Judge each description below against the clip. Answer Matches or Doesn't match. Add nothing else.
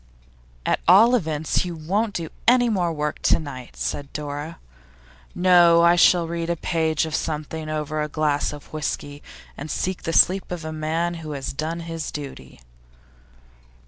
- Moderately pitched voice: Matches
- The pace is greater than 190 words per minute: Doesn't match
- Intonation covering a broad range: Doesn't match